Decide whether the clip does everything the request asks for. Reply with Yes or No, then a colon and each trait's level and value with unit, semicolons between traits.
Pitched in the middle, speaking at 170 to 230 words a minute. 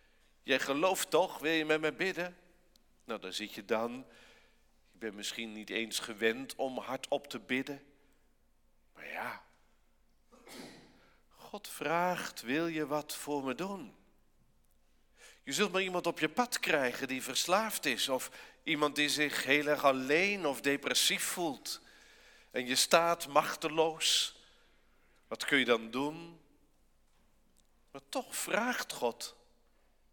No: medium, 145 Hz; slow, 135 wpm